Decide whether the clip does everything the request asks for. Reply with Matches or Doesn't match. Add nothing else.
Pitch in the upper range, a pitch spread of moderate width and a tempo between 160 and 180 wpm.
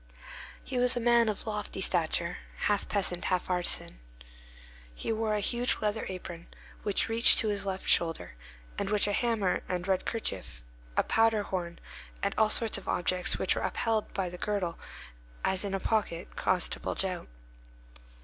Matches